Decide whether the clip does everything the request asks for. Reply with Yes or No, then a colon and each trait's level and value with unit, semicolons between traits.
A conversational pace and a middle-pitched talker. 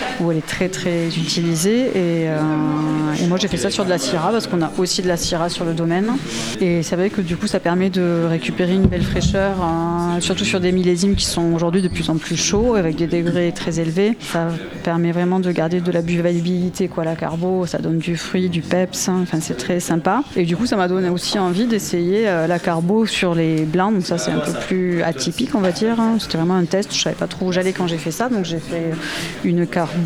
No: fast, 250 wpm; medium, 175 Hz